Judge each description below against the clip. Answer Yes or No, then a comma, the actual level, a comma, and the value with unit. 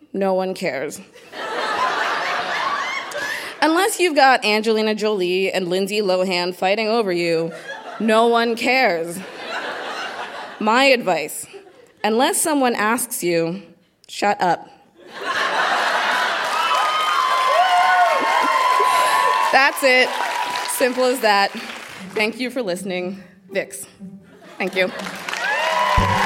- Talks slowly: Yes, slow, 85 wpm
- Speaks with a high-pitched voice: Yes, high, 215 Hz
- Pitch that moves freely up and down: Yes, wide, 5.9 semitones